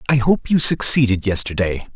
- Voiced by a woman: No, male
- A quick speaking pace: No, average, 155 wpm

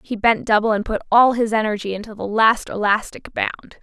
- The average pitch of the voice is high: Yes, high, 215 Hz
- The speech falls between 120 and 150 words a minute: No, fast, 205 wpm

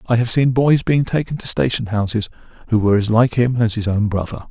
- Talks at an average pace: No, fast, 240 wpm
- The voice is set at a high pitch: No, low, 115 Hz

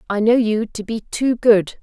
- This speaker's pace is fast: Yes, fast, 230 wpm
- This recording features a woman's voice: Yes, female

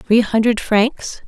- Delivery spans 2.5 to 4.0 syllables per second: Yes, 3.3 syllables/s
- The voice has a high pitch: Yes, high, 225 Hz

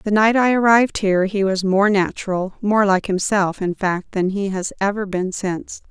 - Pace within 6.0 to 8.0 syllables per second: No, 4.9 syllables/s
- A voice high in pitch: Yes, high, 200 Hz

